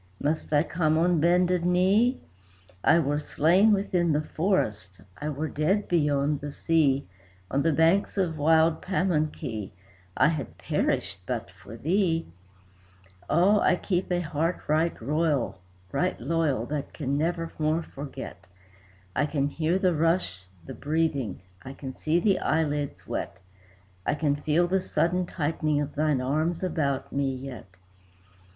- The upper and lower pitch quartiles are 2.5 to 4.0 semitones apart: Yes, average, 3.5 semitones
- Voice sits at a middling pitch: Yes, medium, 155 Hz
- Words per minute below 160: Yes, average, 140 wpm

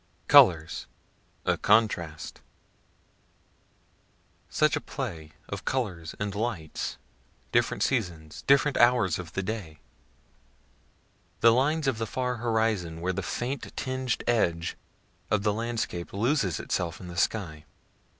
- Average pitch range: No, wide, 5.9 semitones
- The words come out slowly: Yes, slow, 120 wpm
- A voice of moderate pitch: No, low, 105 Hz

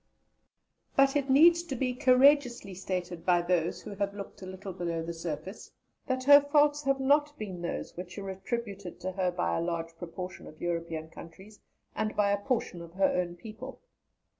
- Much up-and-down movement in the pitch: Yes, wide, 6.8 semitones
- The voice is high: Yes, high, 195 Hz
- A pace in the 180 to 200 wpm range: Yes, average, 185 wpm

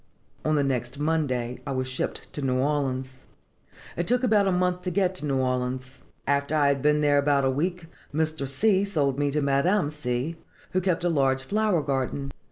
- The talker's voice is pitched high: No, medium, 145 Hz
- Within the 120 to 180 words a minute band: No, average, 195 wpm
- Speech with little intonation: No, average, 4.3 semitones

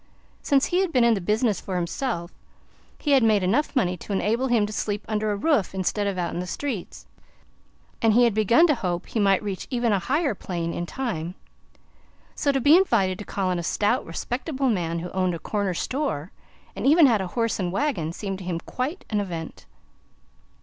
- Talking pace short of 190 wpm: No, fast, 205 wpm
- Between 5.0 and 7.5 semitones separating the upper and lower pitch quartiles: Yes, wide, 5.6 semitones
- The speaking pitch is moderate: No, high, 210 Hz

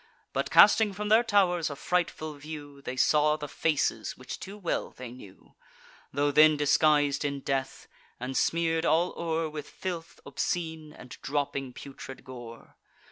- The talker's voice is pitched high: No, medium, 150 Hz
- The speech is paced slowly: No, average, 150 wpm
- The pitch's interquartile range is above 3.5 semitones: No, average, 3.1 semitones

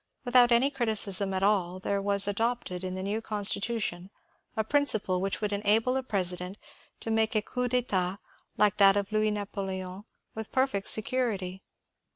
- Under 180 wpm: Yes, average, 160 wpm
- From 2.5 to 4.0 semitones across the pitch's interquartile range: Yes, average, 2.8 semitones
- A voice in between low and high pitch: No, high, 205 Hz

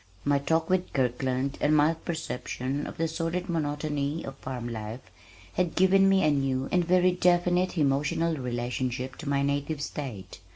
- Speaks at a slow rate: No, average, 160 wpm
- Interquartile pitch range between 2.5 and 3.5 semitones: No, average, 4.1 semitones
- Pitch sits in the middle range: Yes, medium, 145 Hz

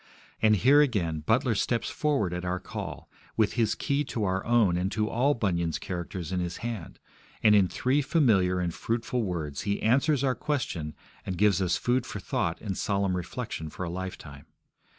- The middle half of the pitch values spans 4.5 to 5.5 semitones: Yes, average, 5.2 semitones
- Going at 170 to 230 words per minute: Yes, average, 185 wpm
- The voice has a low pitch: Yes, low, 100 Hz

